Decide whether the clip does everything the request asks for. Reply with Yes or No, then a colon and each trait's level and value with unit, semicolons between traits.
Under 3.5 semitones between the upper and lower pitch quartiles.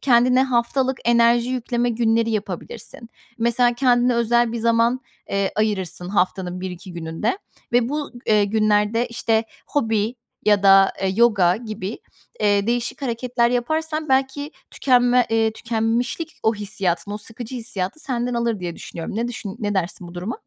Yes: average, 3.0 semitones